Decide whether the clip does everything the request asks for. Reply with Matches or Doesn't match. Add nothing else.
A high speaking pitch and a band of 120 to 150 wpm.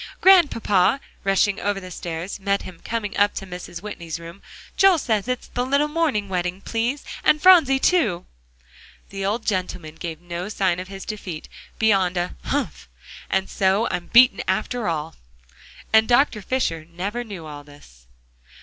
Doesn't match